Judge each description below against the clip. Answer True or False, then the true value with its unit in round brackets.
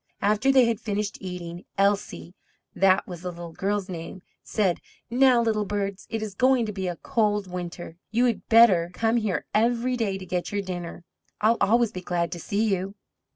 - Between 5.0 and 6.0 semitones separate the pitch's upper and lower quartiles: False (3.7 semitones)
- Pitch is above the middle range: True (200 Hz)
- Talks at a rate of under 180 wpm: False (190 wpm)